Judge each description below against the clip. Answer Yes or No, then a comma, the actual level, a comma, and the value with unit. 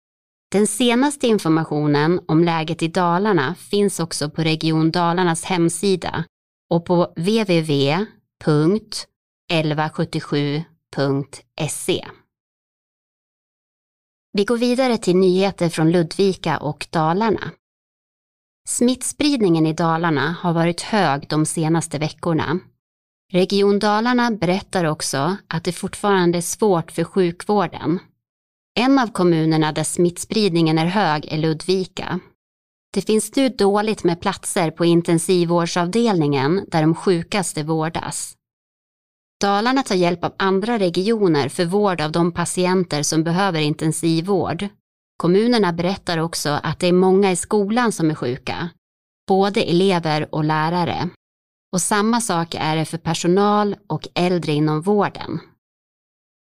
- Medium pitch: Yes, medium, 175 Hz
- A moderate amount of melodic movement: Yes, average, 3.8 semitones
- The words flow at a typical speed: No, slow, 115 wpm